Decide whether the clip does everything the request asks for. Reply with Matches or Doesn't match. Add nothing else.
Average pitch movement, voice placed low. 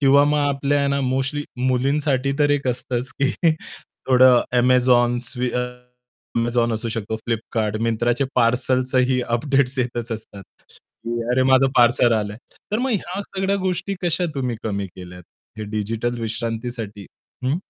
Matches